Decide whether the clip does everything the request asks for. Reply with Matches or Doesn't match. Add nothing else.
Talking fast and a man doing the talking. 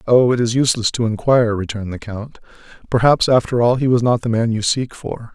Matches